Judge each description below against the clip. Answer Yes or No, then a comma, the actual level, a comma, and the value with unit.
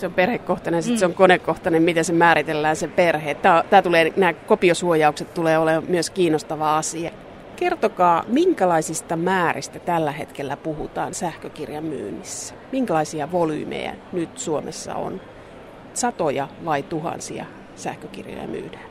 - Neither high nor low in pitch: Yes, medium, 170 Hz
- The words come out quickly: No, average, 125 wpm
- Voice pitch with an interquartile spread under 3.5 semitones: Yes, narrow, 2.4 semitones